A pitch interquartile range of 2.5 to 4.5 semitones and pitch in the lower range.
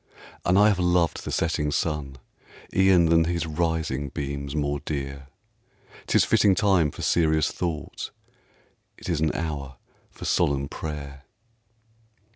Yes: average, 3.2 semitones; very low, 80 Hz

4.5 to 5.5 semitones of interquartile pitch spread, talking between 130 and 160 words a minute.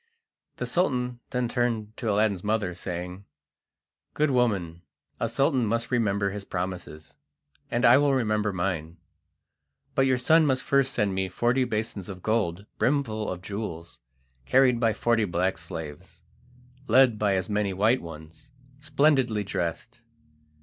Yes: average, 5.0 semitones; average, 140 wpm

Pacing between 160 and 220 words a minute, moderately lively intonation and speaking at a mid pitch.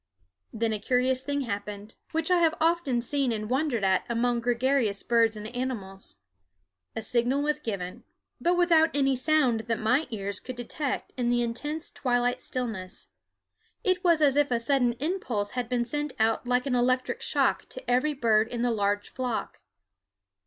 No: average, 170 wpm; average, 4.1 semitones; high, 245 Hz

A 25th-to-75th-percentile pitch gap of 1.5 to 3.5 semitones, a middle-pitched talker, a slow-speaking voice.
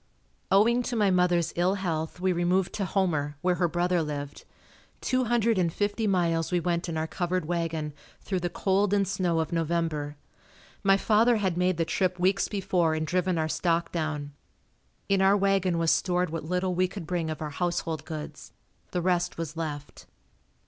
No: narrow, 2.6 semitones; medium, 175 Hz; average, 185 wpm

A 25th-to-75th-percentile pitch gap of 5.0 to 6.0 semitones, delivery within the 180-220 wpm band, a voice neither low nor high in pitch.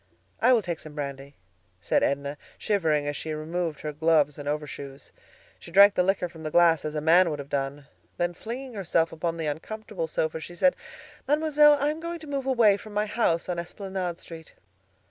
Yes: wide, 5.5 semitones; average, 200 wpm; medium, 170 Hz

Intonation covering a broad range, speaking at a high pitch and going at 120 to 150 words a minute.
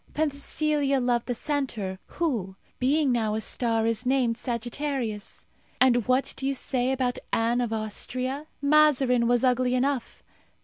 No: average, 2.9 semitones; very high, 250 Hz; average, 140 wpm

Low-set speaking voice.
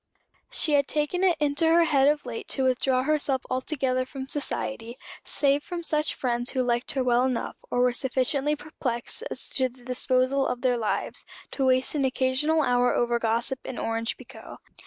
No: very high, 260 Hz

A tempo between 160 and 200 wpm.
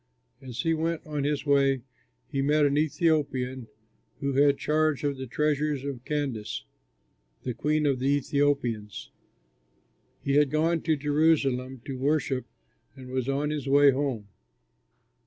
No: average, 140 wpm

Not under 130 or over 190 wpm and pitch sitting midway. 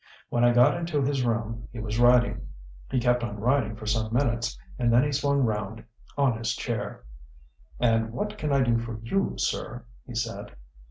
No: average, 185 wpm; low, 120 Hz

